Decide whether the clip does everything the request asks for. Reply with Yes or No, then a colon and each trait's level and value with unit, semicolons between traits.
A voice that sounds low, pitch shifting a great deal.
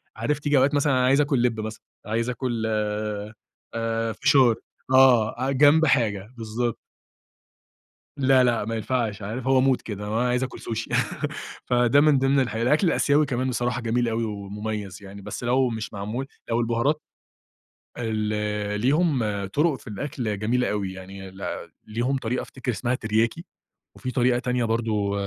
No: low, 120 Hz; average, 3.5 semitones